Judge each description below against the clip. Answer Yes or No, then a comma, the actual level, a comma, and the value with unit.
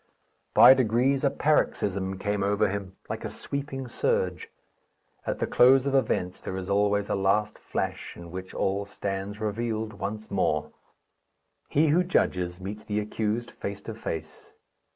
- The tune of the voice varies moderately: Yes, average, 4.1 semitones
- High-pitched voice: No, low, 105 Hz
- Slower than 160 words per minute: Yes, average, 150 wpm